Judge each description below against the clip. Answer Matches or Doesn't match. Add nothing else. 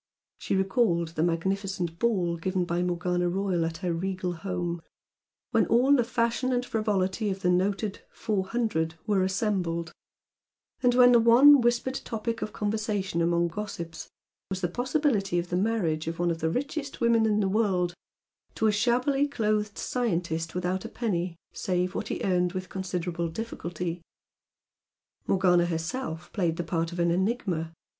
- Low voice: Doesn't match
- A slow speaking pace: Doesn't match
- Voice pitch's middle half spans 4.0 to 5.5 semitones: Matches